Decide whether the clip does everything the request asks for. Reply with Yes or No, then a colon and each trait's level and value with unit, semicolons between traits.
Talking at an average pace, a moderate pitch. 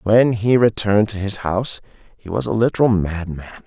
No: average, 180 wpm; low, 105 Hz